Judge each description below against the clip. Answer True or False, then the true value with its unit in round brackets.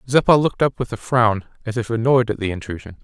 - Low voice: True (115 Hz)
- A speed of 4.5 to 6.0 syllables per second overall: False (6.4 syllables/s)